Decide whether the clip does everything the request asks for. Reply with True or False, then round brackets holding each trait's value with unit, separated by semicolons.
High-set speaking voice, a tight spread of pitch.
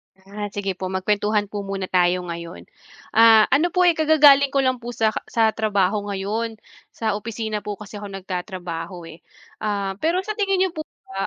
False (210 Hz; 3.9 semitones)